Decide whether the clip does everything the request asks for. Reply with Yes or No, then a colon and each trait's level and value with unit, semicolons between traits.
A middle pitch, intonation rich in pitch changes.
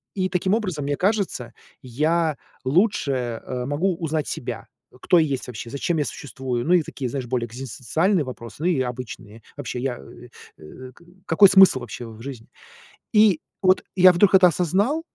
Yes: medium, 145 Hz; wide, 6.6 semitones